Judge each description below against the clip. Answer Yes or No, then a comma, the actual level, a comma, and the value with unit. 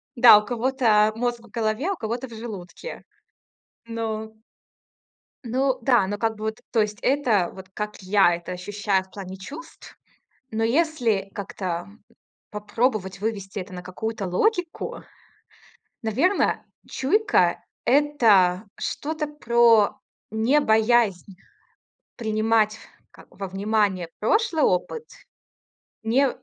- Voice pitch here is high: Yes, high, 220 Hz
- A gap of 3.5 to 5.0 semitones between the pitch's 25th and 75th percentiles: Yes, average, 3.8 semitones